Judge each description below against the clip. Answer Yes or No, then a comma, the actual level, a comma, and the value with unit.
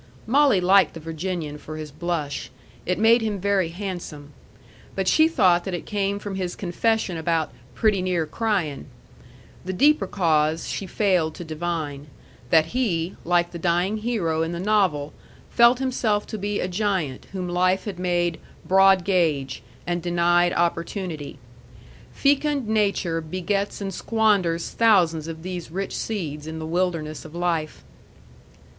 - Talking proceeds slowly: No, average, 150 wpm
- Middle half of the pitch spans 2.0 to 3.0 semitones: No, average, 3.7 semitones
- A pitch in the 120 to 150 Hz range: No, medium, 180 Hz